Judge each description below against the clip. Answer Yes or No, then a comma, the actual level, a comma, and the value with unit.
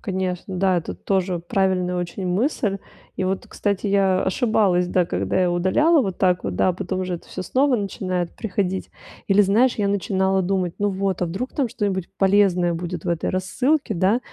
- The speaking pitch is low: No, high, 190 Hz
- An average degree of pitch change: No, narrow, 2.0 semitones